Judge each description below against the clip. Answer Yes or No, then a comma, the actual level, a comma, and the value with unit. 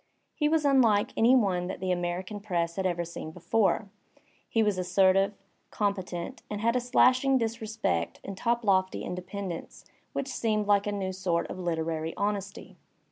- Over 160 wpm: No, average, 155 wpm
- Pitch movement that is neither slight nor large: Yes, average, 3.8 semitones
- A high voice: Yes, high, 195 Hz